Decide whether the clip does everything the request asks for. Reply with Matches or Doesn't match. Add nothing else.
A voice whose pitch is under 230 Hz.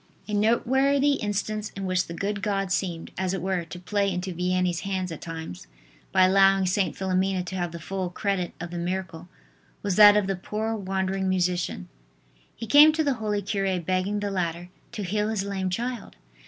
Matches